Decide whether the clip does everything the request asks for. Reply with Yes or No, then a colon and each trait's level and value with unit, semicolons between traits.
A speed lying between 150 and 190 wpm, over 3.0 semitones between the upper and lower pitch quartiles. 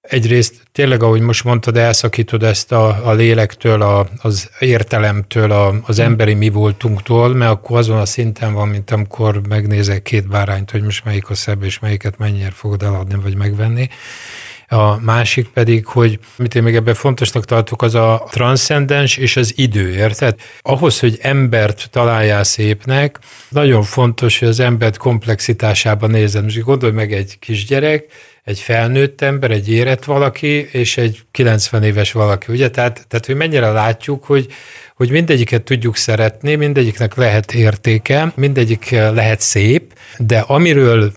No: fast, 155 wpm; average, 2.7 semitones